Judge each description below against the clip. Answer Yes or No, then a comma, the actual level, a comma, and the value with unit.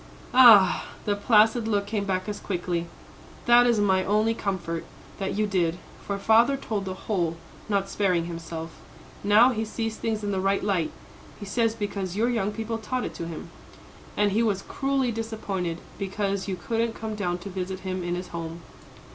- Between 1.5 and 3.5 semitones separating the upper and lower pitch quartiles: Yes, average, 3.1 semitones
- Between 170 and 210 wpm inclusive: Yes, average, 180 wpm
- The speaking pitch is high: Yes, high, 200 Hz